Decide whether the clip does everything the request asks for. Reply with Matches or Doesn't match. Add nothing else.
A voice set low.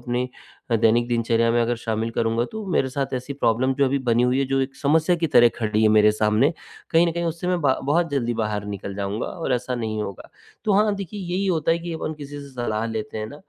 Matches